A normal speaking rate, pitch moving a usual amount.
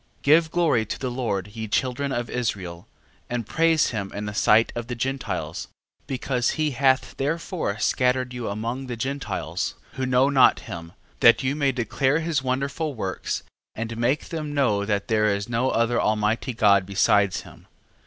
Yes: average, 175 wpm; average, 4.2 semitones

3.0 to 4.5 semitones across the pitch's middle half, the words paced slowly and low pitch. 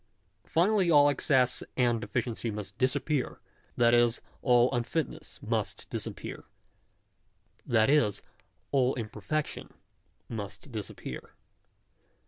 Yes: average, 3.8 semitones; slow, 100 wpm; low, 125 Hz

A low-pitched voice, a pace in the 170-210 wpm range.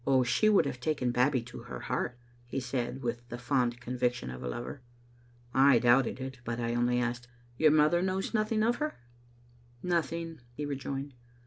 Yes: low, 125 Hz; average, 185 wpm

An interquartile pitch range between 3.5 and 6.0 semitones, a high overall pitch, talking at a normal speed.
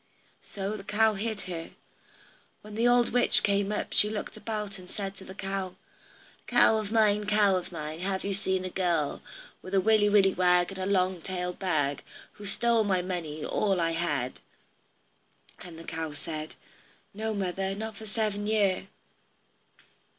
No: average, 2.8 semitones; high, 195 Hz; average, 170 wpm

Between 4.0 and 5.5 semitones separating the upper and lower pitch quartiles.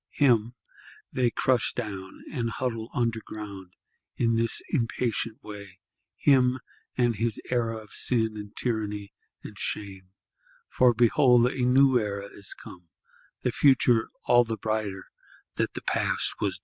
No: average, 3.0 semitones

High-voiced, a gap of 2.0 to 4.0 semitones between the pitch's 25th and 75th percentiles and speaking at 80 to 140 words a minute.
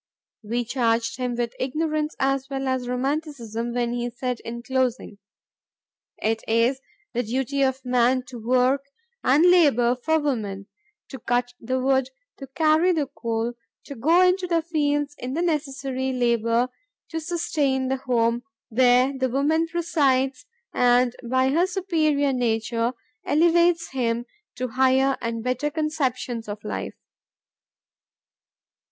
Yes: very high, 260 Hz; average, 3.5 semitones; slow, 135 wpm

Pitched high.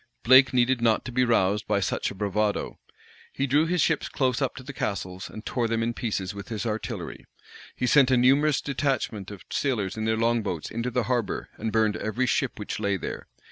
No: low, 115 Hz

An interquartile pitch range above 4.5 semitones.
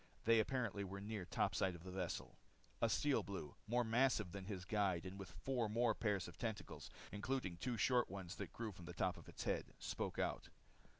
No: average, 3.7 semitones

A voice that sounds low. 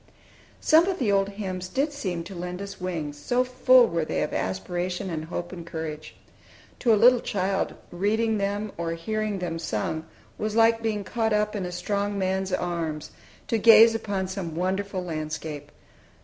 No: high, 190 Hz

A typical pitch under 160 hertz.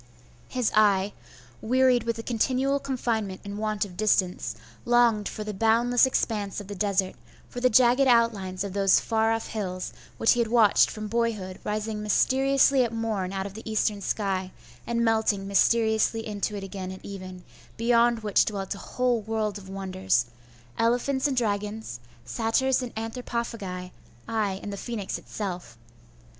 No: high, 215 Hz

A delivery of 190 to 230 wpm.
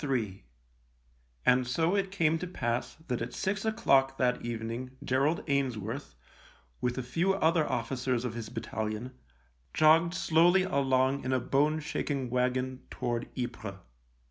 No: average, 140 wpm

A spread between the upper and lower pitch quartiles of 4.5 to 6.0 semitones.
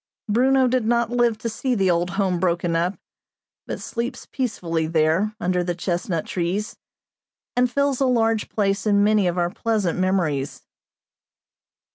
Yes: average, 5.2 semitones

